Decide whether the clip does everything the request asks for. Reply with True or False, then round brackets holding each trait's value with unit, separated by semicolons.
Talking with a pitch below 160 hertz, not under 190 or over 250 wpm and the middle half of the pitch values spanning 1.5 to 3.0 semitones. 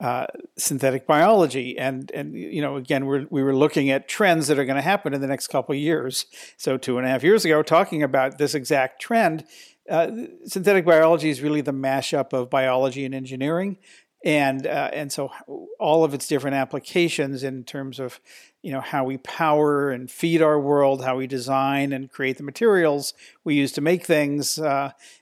True (140 Hz; 195 wpm; 2.6 semitones)